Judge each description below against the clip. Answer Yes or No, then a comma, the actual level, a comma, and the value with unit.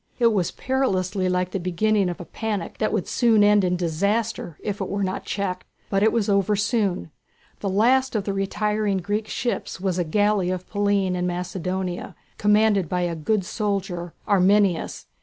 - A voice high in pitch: Yes, high, 195 Hz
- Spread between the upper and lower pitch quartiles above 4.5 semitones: No, narrow, 2.6 semitones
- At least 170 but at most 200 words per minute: Yes, average, 175 wpm